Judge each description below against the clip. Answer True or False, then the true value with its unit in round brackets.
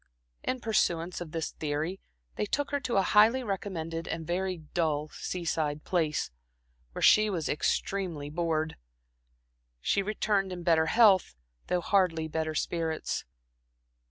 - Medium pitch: True (175 Hz)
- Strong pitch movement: False (3.6 semitones)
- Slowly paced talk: True (130 wpm)